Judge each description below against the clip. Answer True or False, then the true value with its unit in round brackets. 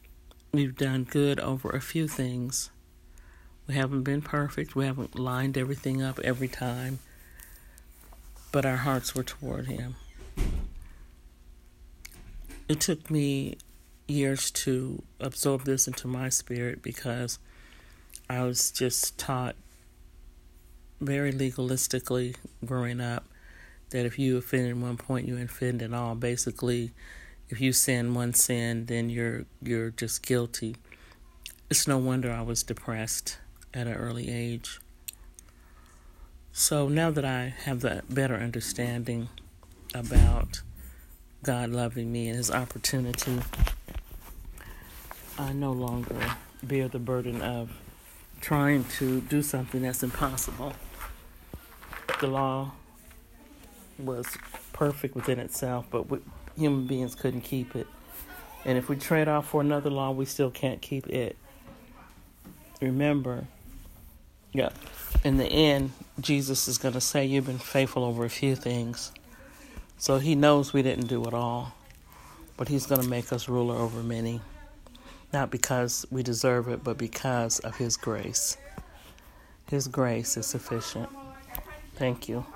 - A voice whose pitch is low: True (125 Hz)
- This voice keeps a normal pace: False (130 wpm)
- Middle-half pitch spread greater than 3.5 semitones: False (2.7 semitones)